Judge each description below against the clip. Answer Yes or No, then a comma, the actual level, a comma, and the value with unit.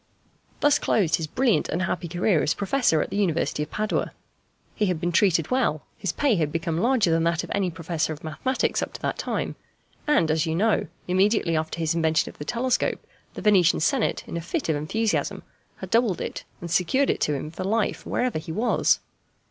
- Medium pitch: Yes, medium, 175 Hz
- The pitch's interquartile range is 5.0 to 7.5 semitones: Yes, wide, 5.5 semitones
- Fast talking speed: Yes, fast, 210 wpm